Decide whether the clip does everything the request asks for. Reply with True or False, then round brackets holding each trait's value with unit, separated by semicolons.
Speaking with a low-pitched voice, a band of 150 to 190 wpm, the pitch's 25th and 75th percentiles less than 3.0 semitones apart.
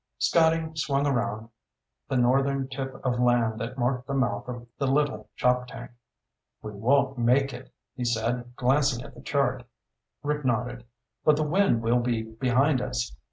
True (125 Hz; 160 wpm; 2.4 semitones)